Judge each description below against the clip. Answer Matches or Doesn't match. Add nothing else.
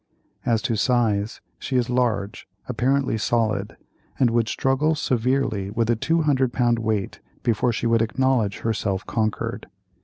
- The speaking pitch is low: Matches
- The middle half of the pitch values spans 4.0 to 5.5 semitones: Doesn't match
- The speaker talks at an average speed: Doesn't match